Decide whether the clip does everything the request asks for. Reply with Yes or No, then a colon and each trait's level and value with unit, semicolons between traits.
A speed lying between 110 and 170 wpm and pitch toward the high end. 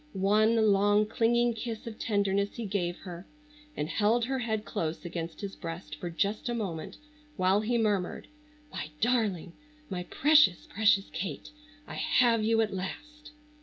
Yes: average, 155 wpm; high, 205 Hz